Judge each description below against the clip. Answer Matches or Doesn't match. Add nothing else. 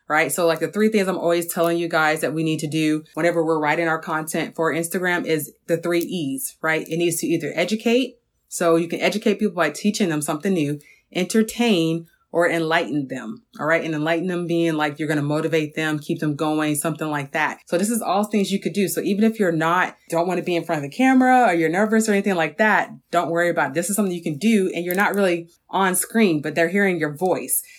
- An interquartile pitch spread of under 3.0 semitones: Doesn't match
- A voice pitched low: Doesn't match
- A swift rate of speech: Matches